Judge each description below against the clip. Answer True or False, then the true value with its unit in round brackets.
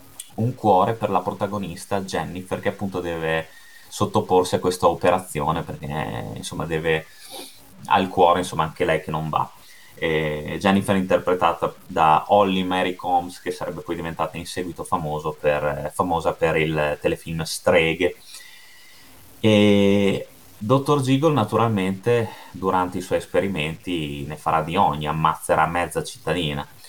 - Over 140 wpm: False (130 wpm)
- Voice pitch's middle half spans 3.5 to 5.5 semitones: True (3.9 semitones)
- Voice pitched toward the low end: True (90 Hz)